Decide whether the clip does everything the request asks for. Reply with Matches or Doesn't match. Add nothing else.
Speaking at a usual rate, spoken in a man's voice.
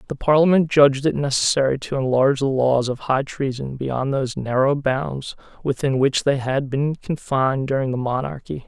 Matches